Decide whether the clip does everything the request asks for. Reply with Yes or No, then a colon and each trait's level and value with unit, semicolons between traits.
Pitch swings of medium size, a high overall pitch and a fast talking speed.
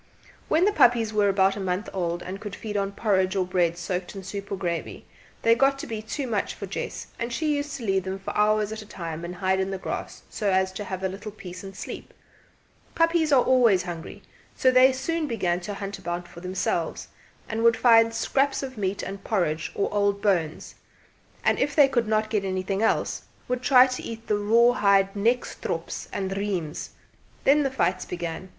Yes: average, 3.7 semitones; high, 200 Hz; fast, 210 wpm